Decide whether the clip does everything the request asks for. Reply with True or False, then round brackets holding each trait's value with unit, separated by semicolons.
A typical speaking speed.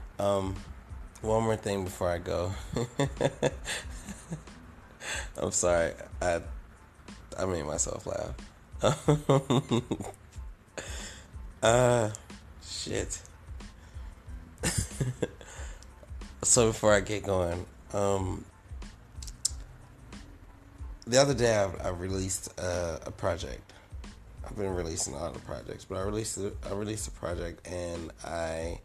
False (100 wpm)